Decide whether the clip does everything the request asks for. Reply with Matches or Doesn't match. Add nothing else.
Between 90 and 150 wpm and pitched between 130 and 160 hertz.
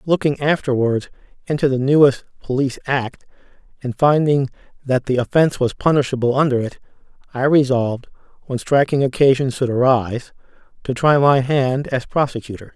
Matches